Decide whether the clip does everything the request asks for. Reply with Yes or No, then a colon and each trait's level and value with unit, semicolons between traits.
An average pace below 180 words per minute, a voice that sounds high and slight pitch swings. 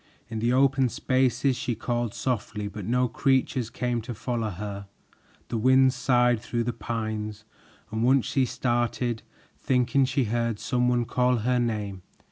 No: average, 155 wpm; low, 120 Hz; narrow, 2.3 semitones